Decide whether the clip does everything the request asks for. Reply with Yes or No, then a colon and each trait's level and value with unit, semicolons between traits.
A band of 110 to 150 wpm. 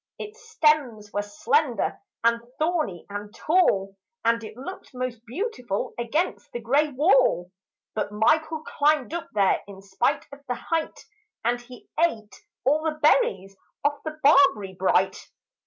Yes: average, 140 wpm